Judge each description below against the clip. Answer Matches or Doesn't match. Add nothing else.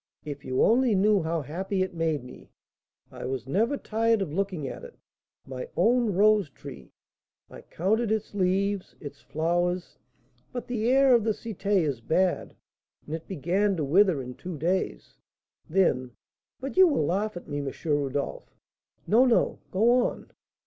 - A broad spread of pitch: Matches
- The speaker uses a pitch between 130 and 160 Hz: Doesn't match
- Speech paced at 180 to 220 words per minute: Doesn't match